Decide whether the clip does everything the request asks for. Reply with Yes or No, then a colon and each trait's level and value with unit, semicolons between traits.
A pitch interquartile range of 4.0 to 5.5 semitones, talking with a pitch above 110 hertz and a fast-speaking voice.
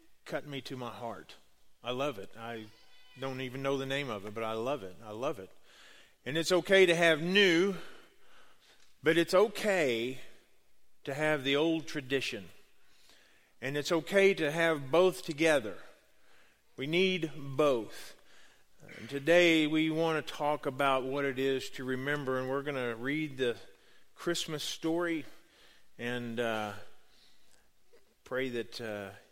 No: average, 4.9 semitones; medium, 140 Hz; average, 145 wpm